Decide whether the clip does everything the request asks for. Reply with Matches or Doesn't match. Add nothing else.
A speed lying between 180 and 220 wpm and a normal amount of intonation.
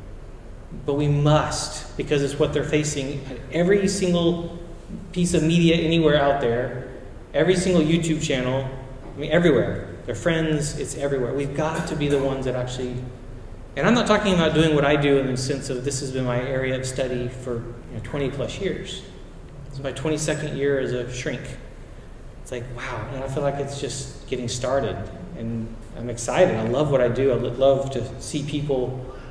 Matches